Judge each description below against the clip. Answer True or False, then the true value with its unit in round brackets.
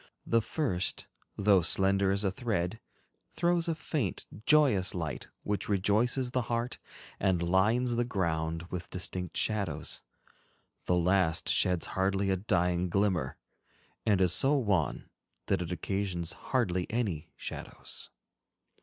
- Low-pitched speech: True (95 Hz)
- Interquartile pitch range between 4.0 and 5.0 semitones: True (4.4 semitones)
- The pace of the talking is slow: True (125 wpm)